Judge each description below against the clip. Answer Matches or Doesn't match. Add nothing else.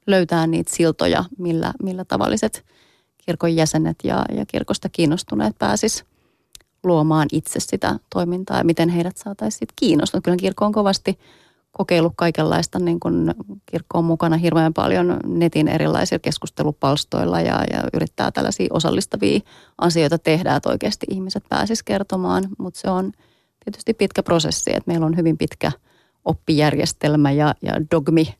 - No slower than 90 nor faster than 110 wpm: Doesn't match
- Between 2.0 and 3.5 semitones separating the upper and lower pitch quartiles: Matches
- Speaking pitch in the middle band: Matches